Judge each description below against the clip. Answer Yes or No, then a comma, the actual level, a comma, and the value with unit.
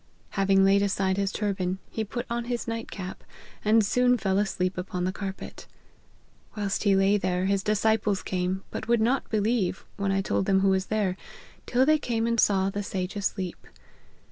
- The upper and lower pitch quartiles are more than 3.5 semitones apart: No, narrow, 2.5 semitones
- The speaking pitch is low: No, high, 200 Hz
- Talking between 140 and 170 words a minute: No, average, 185 wpm